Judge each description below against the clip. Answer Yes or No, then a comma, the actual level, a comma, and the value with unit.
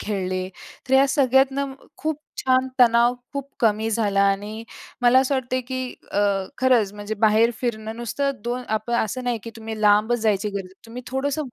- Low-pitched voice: No, high, 235 Hz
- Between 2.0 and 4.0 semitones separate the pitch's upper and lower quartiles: Yes, average, 3.5 semitones